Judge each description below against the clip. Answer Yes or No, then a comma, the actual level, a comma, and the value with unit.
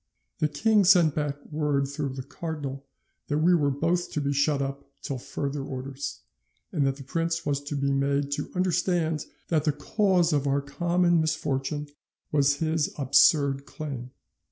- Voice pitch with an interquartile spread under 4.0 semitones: Yes, average, 2.7 semitones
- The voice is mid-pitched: Yes, medium, 145 Hz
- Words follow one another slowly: No, average, 165 wpm